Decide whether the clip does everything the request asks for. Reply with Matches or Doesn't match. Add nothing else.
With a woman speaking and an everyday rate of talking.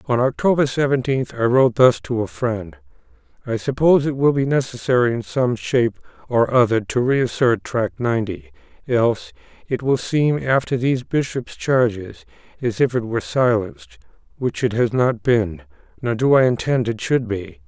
Doesn't match